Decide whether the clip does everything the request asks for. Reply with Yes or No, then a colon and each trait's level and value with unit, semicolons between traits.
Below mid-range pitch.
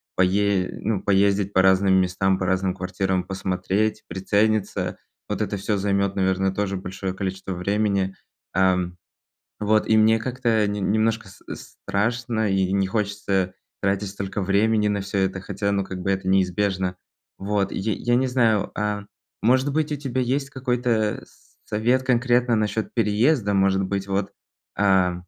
Yes: low, 100 Hz